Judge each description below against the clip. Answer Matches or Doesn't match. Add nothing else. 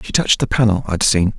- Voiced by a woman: Doesn't match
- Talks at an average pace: Doesn't match